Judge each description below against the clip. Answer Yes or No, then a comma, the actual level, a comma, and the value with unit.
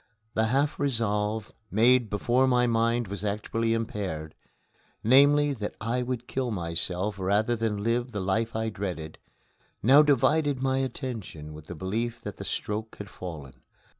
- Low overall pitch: Yes, low, 110 Hz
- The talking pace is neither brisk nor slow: Yes, average, 150 wpm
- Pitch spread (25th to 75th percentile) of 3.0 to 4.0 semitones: Yes, average, 3.7 semitones